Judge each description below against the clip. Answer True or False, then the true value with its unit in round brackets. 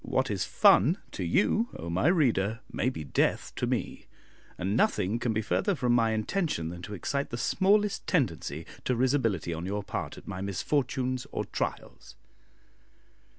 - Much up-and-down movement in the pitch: True (6.6 semitones)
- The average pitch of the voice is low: True (115 Hz)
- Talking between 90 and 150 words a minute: False (165 wpm)